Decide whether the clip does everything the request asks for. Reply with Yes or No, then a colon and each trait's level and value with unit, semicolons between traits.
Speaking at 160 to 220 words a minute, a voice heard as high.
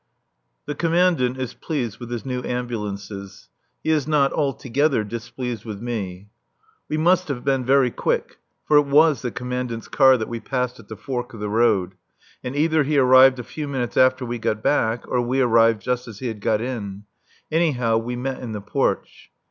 No: average, 190 wpm; low, 125 Hz